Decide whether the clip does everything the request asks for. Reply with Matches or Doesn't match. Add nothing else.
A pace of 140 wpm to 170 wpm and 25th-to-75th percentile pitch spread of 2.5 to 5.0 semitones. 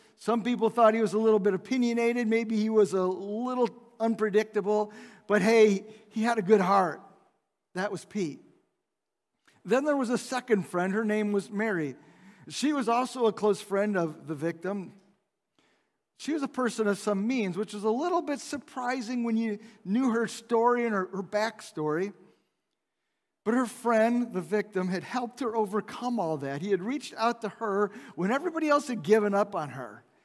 Doesn't match